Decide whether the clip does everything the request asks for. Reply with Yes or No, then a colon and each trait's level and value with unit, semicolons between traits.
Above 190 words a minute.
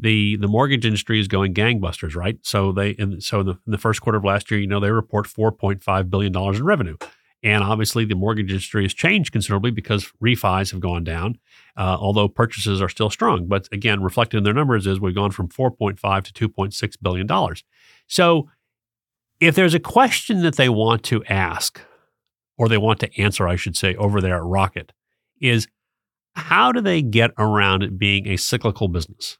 Yes: fast, 205 wpm